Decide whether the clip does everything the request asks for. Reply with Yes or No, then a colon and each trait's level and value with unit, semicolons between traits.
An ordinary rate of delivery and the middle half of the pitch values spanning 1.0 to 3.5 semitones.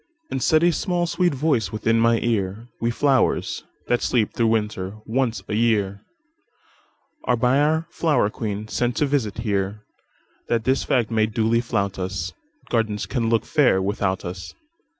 No: average, 145 wpm; average, 4.5 semitones